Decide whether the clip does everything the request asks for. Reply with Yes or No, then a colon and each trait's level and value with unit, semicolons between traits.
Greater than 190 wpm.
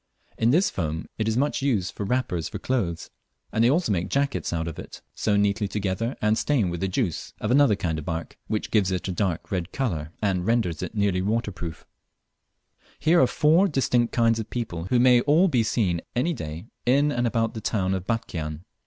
Yes: fast, 205 wpm